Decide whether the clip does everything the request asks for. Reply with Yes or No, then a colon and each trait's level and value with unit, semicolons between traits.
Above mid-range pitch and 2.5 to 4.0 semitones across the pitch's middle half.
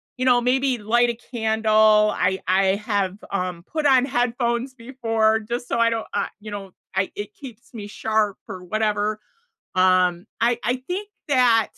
Yes: high, 220 Hz; average, 2.9 semitones